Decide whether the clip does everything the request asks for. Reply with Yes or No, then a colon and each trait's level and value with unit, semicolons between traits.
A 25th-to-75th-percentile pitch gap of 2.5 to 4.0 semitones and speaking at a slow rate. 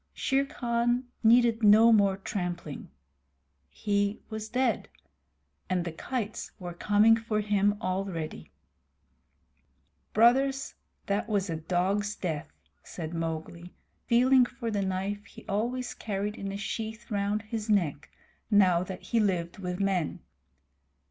Yes: average, 3.6 semitones; slow, 125 wpm